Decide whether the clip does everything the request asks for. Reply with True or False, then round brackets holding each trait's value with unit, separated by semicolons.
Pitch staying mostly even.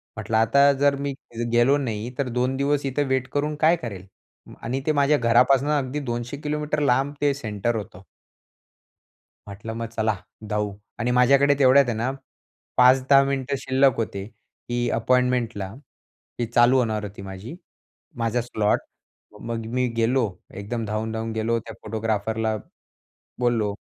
False (3.5 semitones)